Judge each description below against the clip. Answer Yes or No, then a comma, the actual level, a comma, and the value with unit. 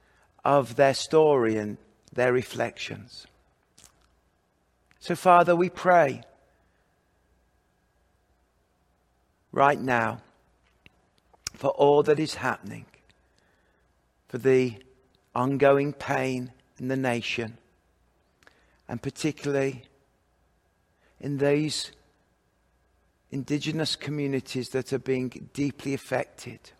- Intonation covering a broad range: Yes, wide, 6.6 semitones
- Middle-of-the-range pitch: No, low, 130 Hz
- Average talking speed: No, slow, 80 wpm